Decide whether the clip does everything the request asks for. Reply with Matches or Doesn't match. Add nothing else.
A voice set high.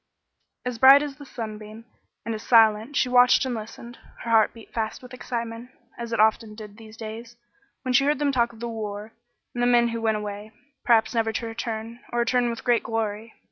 Matches